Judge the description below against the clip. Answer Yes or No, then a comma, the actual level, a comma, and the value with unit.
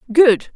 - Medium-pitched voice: No, very high, 255 Hz